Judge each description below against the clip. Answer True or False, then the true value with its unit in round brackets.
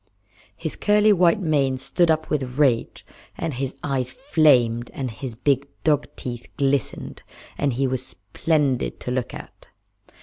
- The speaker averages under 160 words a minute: True (145 wpm)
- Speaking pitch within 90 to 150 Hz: True (135 Hz)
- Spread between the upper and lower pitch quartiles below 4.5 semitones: True (3.8 semitones)